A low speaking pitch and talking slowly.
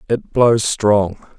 Yes: low, 110 Hz; slow, 130 wpm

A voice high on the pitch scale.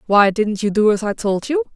Yes: high, 220 Hz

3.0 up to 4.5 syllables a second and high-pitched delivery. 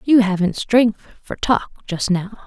Yes: 4.0 syllables/s; high, 210 Hz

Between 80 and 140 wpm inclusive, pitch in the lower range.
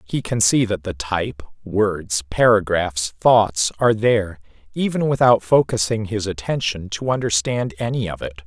No: average, 150 wpm; low, 105 Hz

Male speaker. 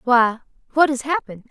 No: female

